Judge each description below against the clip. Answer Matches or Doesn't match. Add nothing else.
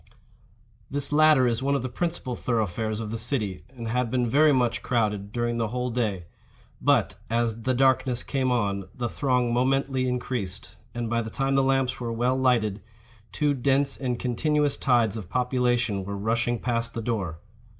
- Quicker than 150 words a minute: Matches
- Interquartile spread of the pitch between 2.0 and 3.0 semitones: Matches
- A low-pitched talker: Matches